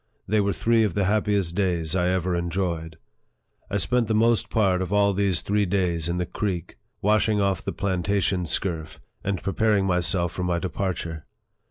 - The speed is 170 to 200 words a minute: Yes, average, 175 wpm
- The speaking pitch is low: Yes, very low, 95 Hz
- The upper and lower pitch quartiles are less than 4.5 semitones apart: Yes, average, 2.8 semitones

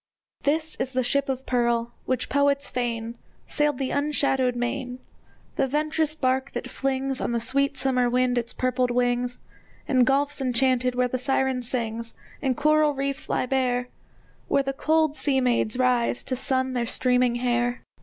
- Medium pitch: No, very high, 255 Hz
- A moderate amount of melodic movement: No, narrow, 2.0 semitones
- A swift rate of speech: No, average, 165 wpm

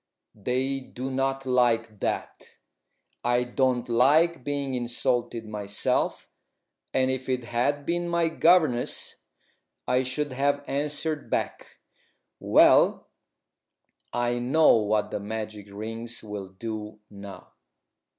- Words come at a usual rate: No, slow, 110 wpm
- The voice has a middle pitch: No, low, 125 Hz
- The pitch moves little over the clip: No, average, 3.6 semitones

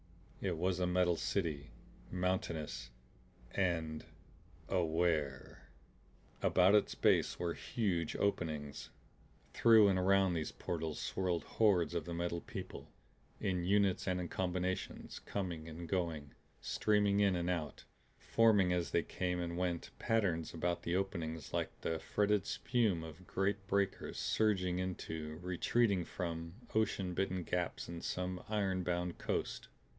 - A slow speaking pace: Yes, slow, 130 wpm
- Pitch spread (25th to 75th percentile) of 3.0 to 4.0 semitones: No, narrow, 2.6 semitones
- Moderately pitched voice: No, very low, 90 Hz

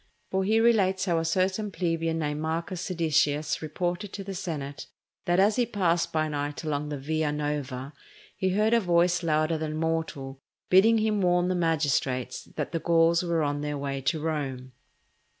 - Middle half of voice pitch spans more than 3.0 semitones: Yes, average, 3.8 semitones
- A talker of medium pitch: Yes, medium, 165 Hz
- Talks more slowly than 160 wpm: No, average, 175 wpm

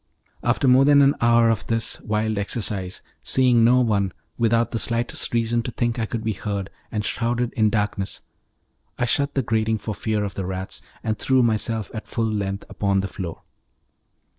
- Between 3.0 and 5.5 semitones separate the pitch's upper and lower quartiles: No, narrow, 2.4 semitones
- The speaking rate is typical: Yes, average, 185 wpm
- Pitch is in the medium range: No, low, 110 Hz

